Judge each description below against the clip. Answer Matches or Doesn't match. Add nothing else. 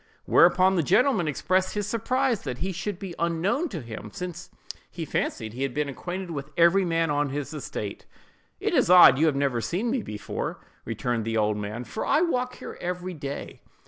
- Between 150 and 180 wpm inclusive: Doesn't match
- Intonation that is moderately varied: Doesn't match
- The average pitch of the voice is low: Doesn't match